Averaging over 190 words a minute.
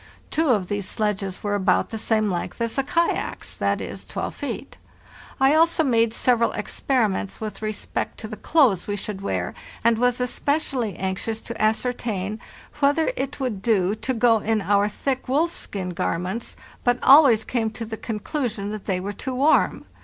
No: average, 170 wpm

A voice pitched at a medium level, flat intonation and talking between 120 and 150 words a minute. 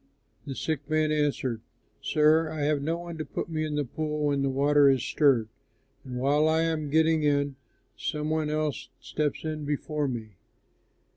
No: medium, 150 Hz; narrow, 1.7 semitones; average, 175 wpm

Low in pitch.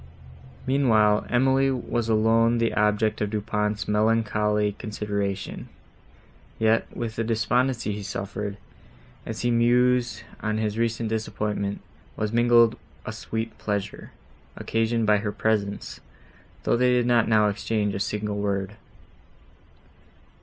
Yes: low, 110 Hz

